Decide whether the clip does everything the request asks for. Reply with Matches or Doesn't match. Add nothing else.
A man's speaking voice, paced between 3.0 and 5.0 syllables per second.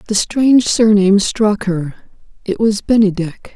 Doesn't match